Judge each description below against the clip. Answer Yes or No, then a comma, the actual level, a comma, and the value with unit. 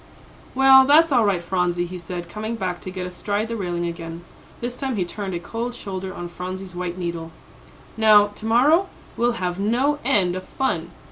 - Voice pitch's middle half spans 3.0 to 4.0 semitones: No, average, 4.8 semitones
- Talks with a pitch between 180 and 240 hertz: Yes, high, 190 Hz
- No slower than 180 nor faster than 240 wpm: Yes, average, 190 wpm